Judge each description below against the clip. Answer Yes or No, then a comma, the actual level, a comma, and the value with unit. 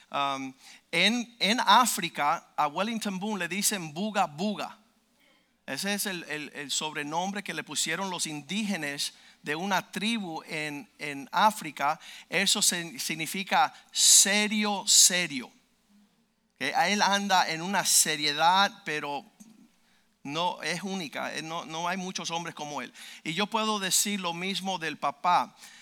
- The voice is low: No, high, 190 Hz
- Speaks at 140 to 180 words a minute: No, average, 130 wpm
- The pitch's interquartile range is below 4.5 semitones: No, average, 4.9 semitones